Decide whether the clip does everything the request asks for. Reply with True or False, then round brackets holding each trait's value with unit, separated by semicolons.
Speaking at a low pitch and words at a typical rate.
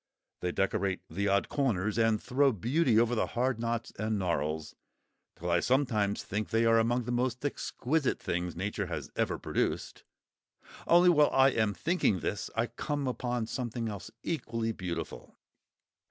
True (115 Hz; 155 wpm)